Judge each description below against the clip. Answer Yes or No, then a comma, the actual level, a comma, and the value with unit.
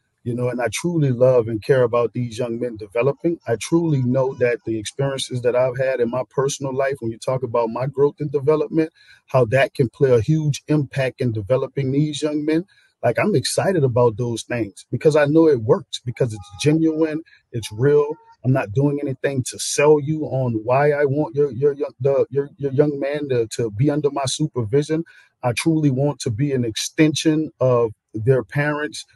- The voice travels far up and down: No, average, 3.2 semitones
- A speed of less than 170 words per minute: No, average, 200 wpm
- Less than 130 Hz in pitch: No, low, 135 Hz